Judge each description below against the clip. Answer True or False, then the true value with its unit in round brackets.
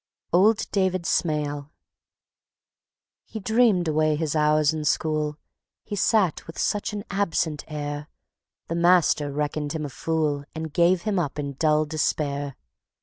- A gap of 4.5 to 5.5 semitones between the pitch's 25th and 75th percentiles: False (3.3 semitones)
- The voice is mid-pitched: True (155 Hz)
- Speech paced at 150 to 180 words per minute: False (140 wpm)